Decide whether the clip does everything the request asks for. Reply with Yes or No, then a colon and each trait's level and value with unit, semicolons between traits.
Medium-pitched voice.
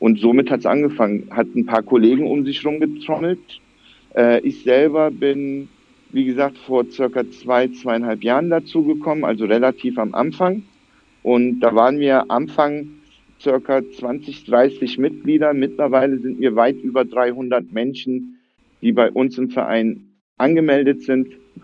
No: low, 130 Hz